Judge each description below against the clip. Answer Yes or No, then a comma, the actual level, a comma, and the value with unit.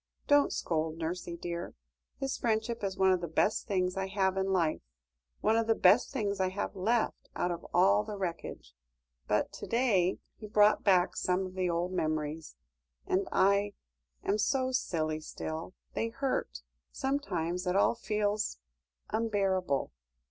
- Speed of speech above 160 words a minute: No, average, 155 wpm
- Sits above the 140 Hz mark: Yes, high, 190 Hz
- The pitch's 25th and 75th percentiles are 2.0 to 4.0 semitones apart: Yes, average, 3.6 semitones